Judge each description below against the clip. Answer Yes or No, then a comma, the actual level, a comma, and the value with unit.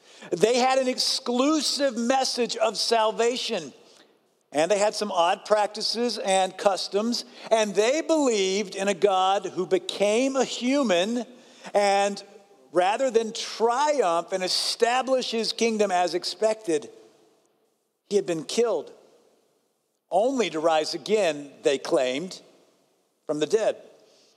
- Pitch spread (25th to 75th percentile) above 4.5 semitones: Yes, average, 5.0 semitones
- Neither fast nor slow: No, slow, 120 wpm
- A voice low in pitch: No, high, 215 Hz